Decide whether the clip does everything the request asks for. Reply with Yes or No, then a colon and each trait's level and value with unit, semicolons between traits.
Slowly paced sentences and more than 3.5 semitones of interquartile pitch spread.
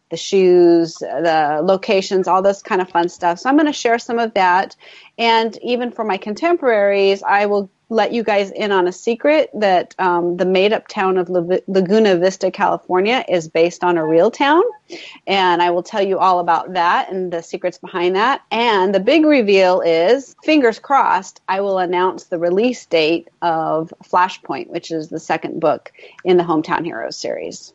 No: average, 190 wpm; average, 3.9 semitones